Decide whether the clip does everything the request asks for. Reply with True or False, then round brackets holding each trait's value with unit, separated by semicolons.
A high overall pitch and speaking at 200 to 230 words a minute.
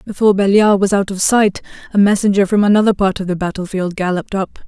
True (195 Hz; 205 wpm)